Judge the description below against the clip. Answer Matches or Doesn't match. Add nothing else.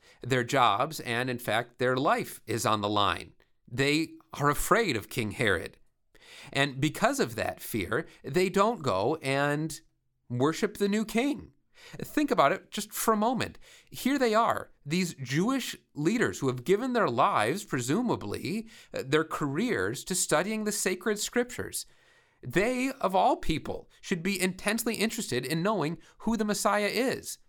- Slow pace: Doesn't match